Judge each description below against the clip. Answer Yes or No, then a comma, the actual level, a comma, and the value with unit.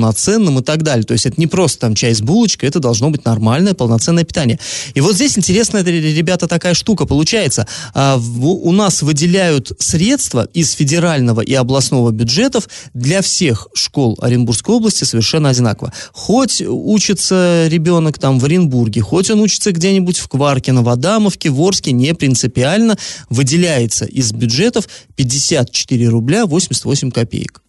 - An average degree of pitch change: No, wide, 6.6 semitones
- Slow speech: No, average, 150 wpm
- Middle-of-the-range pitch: Yes, medium, 150 Hz